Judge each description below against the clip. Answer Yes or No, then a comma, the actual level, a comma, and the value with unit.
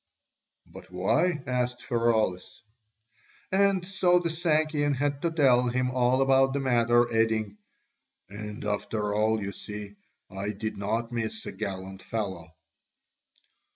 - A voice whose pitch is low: Yes, low, 120 Hz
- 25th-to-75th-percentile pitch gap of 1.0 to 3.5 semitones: No, average, 4.6 semitones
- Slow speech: Yes, slow, 125 wpm